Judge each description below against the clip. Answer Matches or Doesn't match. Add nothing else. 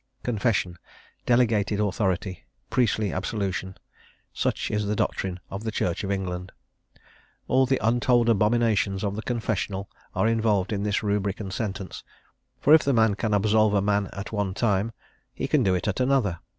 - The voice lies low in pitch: Matches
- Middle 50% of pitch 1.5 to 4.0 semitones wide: Matches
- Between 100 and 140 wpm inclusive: Doesn't match